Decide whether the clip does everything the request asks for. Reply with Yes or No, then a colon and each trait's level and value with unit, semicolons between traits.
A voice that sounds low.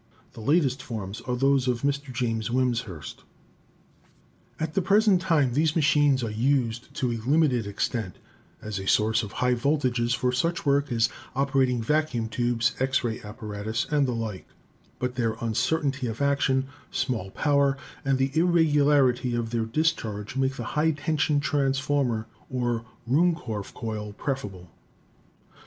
Yes: low, 125 Hz